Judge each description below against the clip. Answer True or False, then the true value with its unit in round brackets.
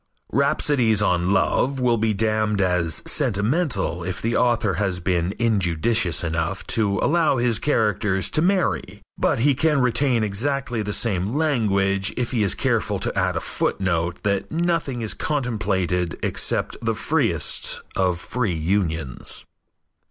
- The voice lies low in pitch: True (105 Hz)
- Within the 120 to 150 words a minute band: True (140 wpm)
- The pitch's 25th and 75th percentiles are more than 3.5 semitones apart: True (5.0 semitones)